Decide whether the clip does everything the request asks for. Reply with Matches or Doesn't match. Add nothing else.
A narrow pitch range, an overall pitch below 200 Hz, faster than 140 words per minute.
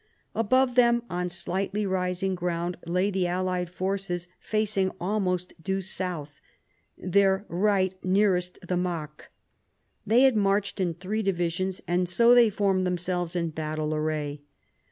Doesn't match